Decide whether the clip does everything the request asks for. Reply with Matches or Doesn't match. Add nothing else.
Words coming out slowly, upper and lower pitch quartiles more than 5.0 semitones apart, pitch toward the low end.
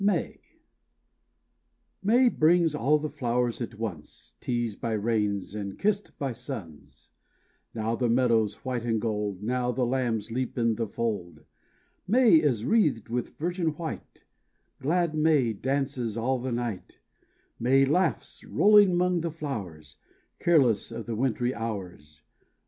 Matches